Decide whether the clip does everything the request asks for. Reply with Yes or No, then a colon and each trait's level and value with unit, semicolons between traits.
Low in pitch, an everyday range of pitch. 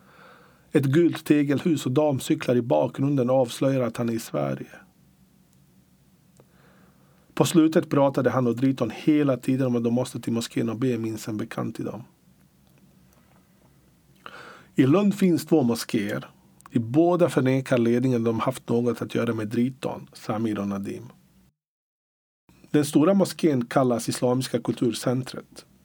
Yes: low, 130 Hz; average, 4.1 semitones